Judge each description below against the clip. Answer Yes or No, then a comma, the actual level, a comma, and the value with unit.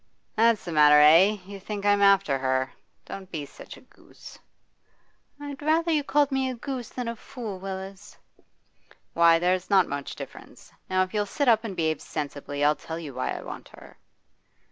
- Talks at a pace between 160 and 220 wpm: Yes, average, 185 wpm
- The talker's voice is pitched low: No, high, 195 Hz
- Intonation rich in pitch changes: Yes, wide, 6.4 semitones